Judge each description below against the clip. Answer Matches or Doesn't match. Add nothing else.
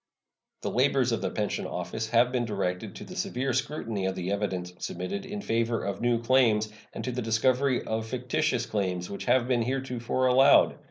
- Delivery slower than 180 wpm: Doesn't match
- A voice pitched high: Doesn't match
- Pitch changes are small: Doesn't match